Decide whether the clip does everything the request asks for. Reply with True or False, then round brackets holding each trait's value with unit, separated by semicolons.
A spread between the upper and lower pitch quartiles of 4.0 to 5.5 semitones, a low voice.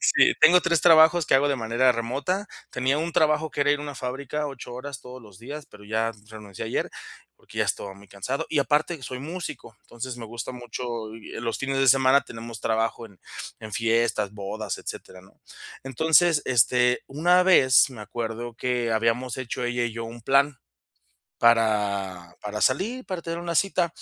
True (4.4 semitones; 125 Hz)